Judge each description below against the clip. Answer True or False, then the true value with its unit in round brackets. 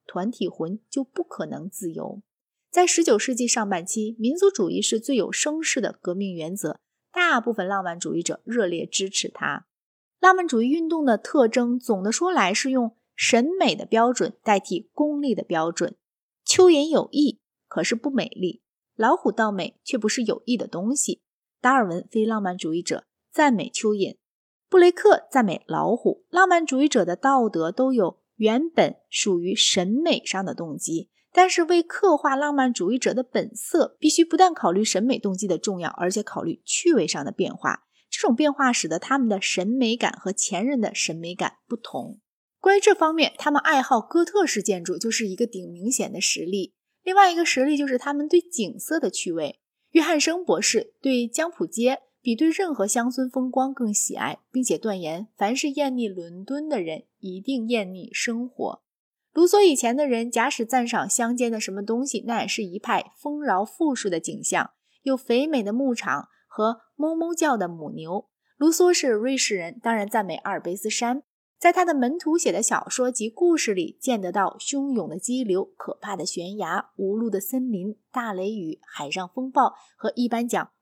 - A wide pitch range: True (6.4 semitones)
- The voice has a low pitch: False (240 Hz)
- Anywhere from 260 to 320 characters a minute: True (270 characters per minute)